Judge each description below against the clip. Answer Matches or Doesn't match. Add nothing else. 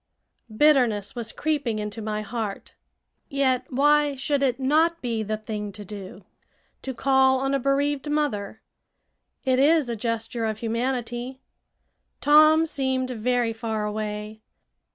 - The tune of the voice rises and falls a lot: Doesn't match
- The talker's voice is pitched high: Matches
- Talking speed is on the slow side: Matches